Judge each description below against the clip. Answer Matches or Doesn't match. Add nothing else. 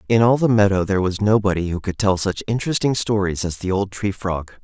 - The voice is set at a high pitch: Doesn't match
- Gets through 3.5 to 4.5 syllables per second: Doesn't match